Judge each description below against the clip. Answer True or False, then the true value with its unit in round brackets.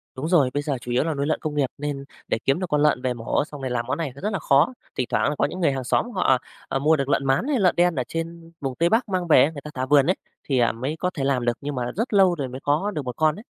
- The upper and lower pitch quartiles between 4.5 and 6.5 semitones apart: False (4.1 semitones)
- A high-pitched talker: False (145 Hz)